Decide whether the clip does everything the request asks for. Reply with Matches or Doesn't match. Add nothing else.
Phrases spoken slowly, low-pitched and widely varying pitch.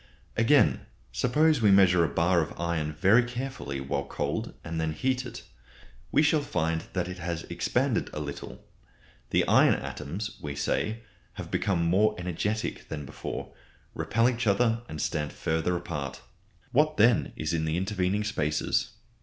Doesn't match